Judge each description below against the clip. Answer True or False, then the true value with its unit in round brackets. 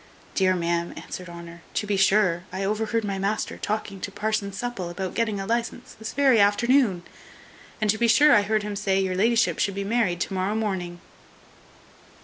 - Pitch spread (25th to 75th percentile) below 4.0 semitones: True (2.8 semitones)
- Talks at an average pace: True (185 wpm)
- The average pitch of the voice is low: False (205 Hz)